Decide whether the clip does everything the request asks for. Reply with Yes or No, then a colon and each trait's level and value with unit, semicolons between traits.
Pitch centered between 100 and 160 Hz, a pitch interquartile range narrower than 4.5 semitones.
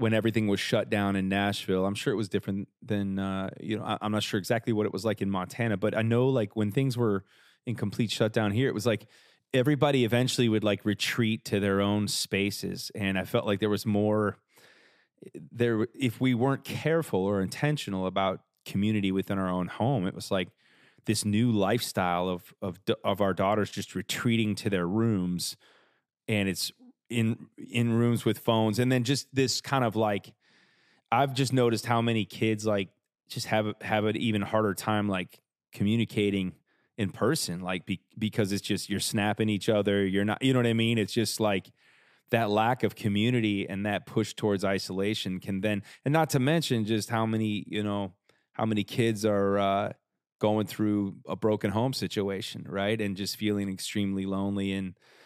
Yes: low, 105 Hz; narrow, 2.6 semitones